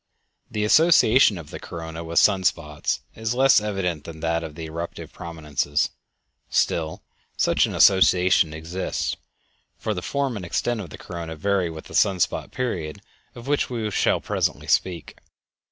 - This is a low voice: Yes, very low, 90 Hz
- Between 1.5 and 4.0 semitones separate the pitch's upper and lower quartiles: No, average, 4.6 semitones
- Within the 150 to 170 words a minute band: Yes, average, 160 wpm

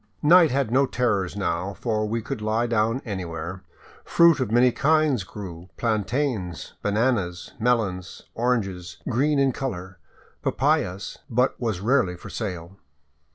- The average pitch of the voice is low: Yes, low, 110 Hz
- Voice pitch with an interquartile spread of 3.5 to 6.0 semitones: Yes, average, 5.3 semitones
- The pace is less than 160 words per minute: Yes, average, 140 wpm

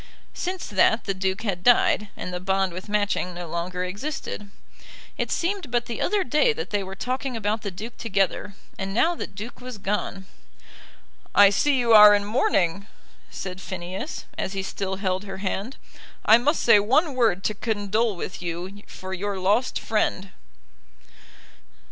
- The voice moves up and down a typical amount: Yes, average, 3.9 semitones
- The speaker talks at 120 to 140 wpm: No, average, 165 wpm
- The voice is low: No, high, 205 Hz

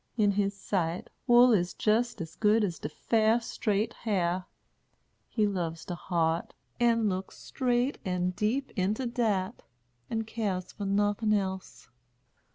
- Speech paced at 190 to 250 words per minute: No, average, 140 wpm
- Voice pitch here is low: No, high, 205 Hz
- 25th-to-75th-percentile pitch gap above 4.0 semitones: No, average, 3.5 semitones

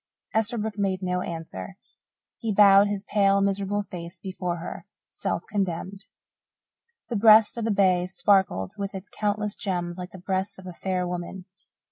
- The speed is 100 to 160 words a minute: Yes, average, 155 wpm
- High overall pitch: Yes, high, 195 Hz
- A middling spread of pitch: No, narrow, 2.2 semitones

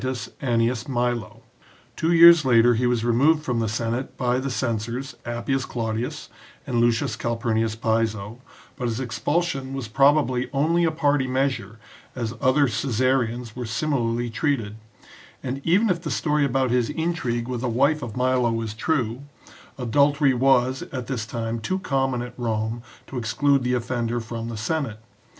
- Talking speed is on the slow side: No, average, 160 wpm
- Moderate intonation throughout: Yes, average, 3.0 semitones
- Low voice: Yes, low, 125 Hz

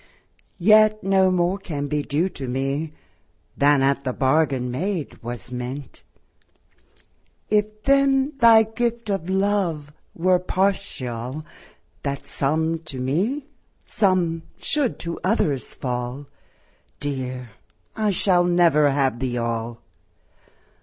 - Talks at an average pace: No, slow, 110 wpm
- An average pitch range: No, wide, 6.7 semitones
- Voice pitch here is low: No, medium, 160 Hz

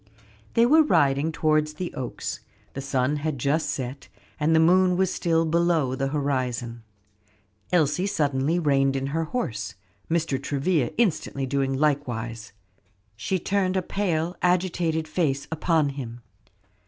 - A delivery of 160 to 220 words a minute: No, slow, 135 wpm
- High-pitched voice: No, medium, 150 Hz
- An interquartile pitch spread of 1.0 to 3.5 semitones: No, average, 4.1 semitones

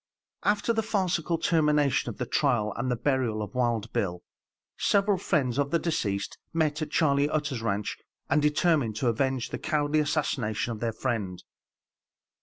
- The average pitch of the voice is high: No, medium, 140 Hz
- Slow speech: No, average, 160 wpm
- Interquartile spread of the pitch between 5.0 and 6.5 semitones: Yes, wide, 5.4 semitones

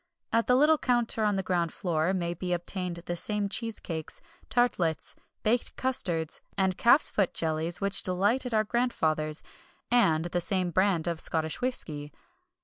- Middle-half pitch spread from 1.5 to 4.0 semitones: No, average, 5.3 semitones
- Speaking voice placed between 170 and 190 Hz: Yes, medium, 185 Hz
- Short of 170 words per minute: Yes, average, 150 wpm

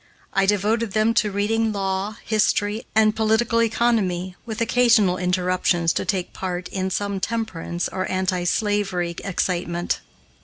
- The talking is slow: Yes, slow, 130 wpm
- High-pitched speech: Yes, high, 200 Hz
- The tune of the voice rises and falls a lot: No, average, 3.1 semitones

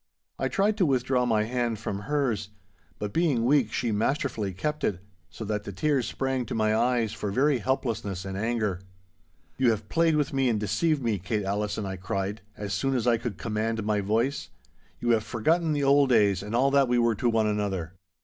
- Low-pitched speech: Yes, low, 115 Hz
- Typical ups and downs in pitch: Yes, average, 4.3 semitones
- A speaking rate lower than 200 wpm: No, fast, 205 wpm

